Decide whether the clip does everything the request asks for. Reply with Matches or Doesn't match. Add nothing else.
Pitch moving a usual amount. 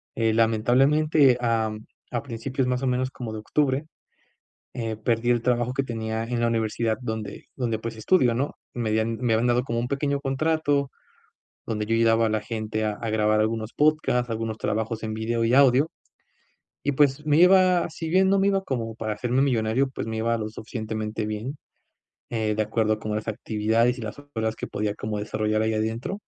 Matches